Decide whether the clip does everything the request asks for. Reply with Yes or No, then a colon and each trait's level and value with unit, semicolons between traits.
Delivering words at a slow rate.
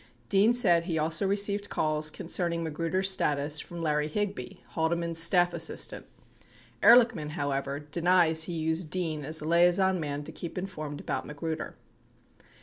No: average, 145 wpm